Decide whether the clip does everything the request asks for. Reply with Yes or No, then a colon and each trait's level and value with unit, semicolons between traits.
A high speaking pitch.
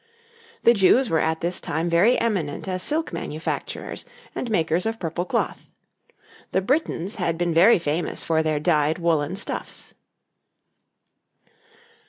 No: medium, 175 Hz